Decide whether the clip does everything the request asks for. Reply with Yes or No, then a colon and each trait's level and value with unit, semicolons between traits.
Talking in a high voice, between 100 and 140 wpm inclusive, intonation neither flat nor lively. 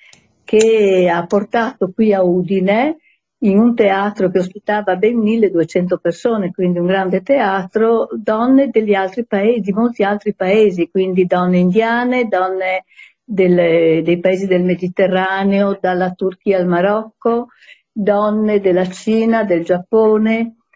Yes: high, 200 Hz; average, 120 wpm; average, 3.1 semitones